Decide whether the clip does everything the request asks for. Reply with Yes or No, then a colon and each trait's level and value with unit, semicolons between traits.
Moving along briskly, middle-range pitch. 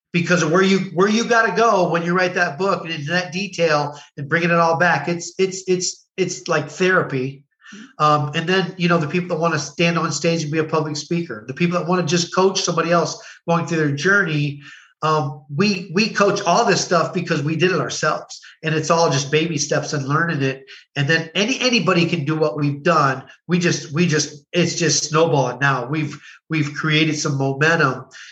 Yes: fast, 220 wpm; medium, 165 Hz